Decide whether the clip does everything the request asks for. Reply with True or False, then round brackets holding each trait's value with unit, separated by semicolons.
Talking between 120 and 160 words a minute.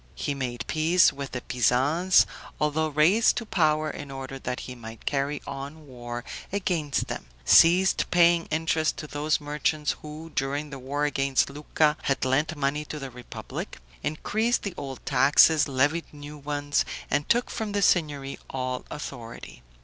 True (155 wpm)